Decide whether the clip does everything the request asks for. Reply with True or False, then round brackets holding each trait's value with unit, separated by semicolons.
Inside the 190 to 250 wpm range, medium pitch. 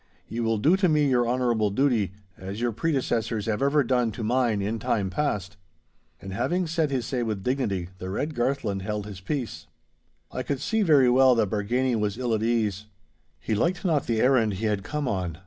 False (200 wpm; 115 Hz)